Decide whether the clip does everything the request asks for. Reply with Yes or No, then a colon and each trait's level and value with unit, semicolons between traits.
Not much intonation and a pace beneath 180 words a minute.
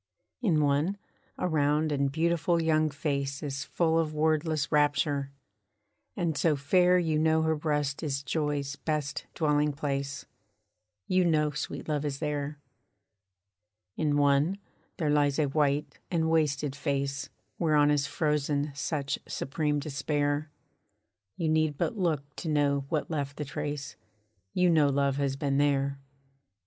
Yes: narrow, 1.9 semitones; average, 140 wpm